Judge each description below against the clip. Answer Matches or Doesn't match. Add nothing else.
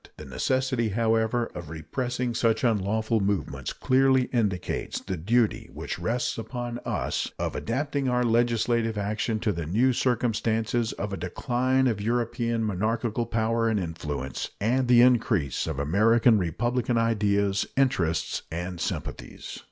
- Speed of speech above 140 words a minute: Doesn't match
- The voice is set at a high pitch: Doesn't match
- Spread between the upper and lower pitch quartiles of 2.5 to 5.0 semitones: Matches